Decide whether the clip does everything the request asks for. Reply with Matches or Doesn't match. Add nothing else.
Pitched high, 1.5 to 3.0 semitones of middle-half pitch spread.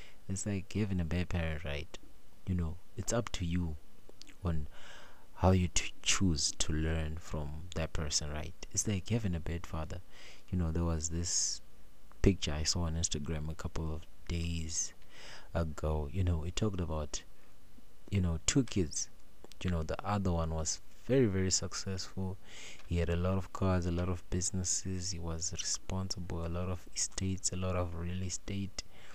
Doesn't match